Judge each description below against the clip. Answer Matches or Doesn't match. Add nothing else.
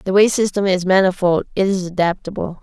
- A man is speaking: Doesn't match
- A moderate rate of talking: Matches